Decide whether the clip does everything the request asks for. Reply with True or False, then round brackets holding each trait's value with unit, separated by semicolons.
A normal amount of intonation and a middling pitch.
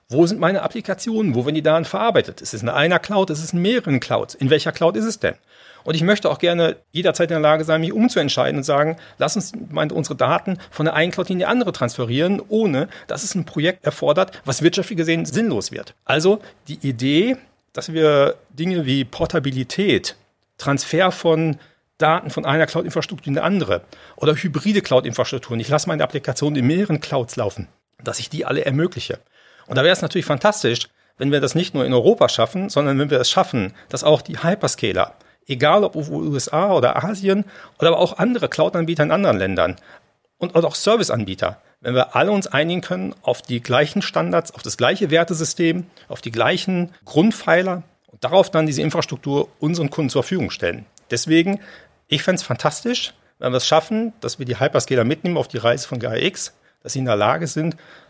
True (4.5 semitones; 160 Hz)